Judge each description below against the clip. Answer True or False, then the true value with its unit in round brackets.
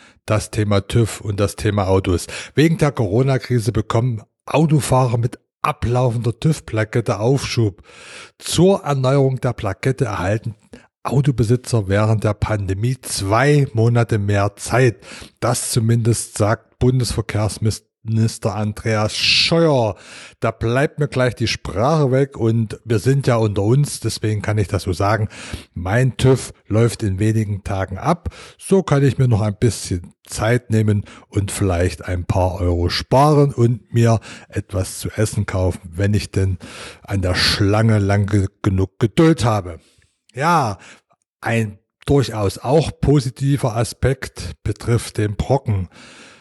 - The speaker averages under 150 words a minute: True (130 wpm)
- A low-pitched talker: True (110 Hz)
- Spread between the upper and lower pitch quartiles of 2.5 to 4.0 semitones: True (3.7 semitones)